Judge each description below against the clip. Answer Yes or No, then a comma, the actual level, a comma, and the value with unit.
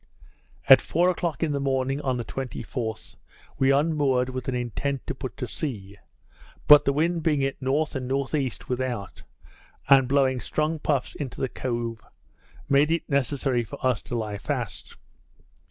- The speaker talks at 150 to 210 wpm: Yes, average, 160 wpm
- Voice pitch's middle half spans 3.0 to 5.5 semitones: No, narrow, 2.4 semitones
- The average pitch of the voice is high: No, low, 135 Hz